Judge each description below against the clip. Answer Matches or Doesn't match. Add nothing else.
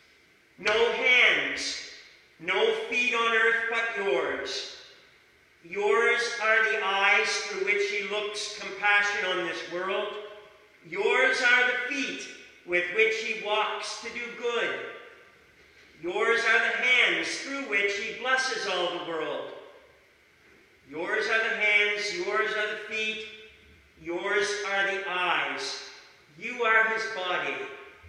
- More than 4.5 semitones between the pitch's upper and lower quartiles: Doesn't match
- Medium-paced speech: Doesn't match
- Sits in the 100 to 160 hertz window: Doesn't match